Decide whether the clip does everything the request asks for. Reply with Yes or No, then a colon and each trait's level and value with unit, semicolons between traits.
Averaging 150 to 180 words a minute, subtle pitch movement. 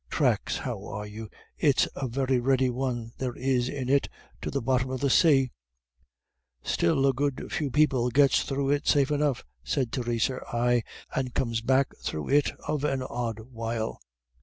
Yes: average, 170 wpm; narrow, 2.3 semitones